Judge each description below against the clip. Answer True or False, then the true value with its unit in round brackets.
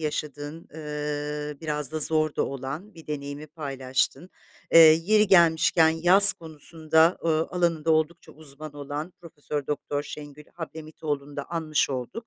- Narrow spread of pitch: True (2.0 semitones)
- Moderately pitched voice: True (155 Hz)